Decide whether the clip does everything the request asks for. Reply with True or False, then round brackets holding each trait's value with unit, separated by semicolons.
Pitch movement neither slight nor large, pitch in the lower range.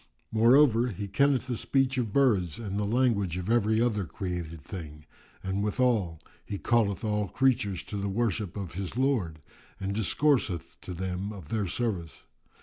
True (4.4 semitones; 105 Hz)